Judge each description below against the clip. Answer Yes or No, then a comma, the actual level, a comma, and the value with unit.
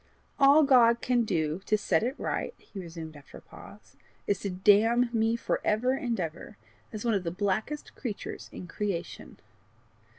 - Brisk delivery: No, average, 170 wpm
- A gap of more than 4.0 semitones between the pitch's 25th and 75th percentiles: Yes, average, 4.8 semitones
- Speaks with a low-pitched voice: No, high, 210 Hz